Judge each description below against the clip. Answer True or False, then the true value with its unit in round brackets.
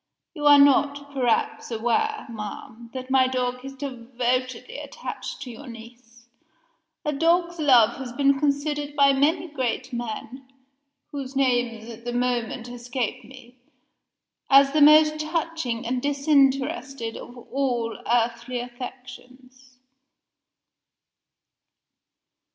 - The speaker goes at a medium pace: False (110 wpm)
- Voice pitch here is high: True (255 Hz)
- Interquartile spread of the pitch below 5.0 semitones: True (2.8 semitones)